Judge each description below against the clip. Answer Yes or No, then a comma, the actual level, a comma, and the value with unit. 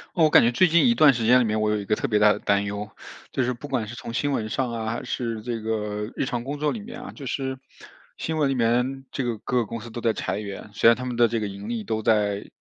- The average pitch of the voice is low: Yes, low, 115 Hz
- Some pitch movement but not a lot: Yes, average, 3.6 semitones